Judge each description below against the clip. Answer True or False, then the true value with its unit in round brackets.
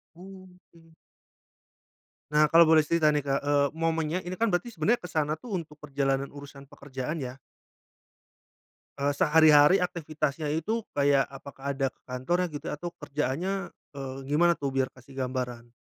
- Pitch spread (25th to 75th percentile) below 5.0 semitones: True (3.5 semitones)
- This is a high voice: False (150 Hz)